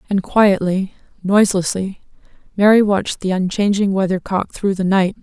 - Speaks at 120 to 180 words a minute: Yes, average, 140 wpm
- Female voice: Yes, female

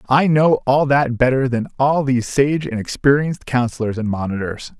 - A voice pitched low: Yes, low, 130 Hz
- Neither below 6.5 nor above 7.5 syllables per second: No, 5.2 syllables/s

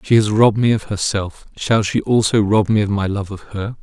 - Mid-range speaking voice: No, low, 105 Hz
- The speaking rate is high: Yes, fast, 250 wpm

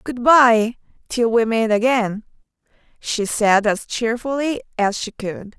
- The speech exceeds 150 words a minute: No, average, 140 wpm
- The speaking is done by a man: No, female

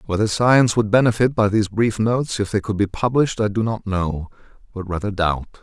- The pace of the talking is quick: Yes, fast, 215 wpm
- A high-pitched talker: No, low, 105 Hz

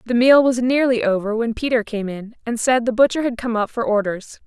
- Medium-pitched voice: No, high, 235 Hz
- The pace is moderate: No, fast, 240 wpm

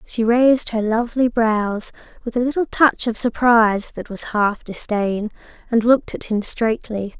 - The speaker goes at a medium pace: Yes, average, 165 wpm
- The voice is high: Yes, high, 230 Hz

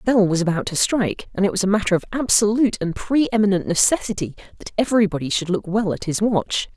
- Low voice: No, high, 200 Hz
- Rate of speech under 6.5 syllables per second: No, 6.6 syllables/s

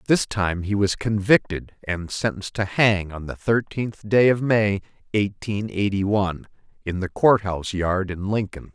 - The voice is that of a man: Yes, male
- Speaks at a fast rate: No, average, 170 wpm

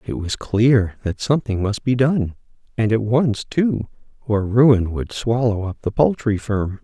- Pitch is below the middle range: Yes, low, 115 Hz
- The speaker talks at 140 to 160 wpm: No, average, 175 wpm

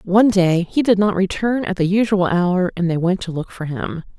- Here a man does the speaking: No, female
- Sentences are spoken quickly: Yes, fast, 245 wpm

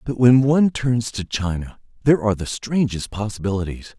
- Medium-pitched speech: No, low, 115 Hz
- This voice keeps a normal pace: Yes, average, 165 wpm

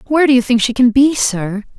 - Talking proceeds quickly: Yes, fast, 270 wpm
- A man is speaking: No, female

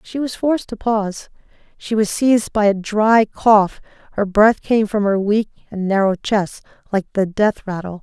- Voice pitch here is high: Yes, high, 210 Hz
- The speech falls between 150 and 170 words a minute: No, average, 185 wpm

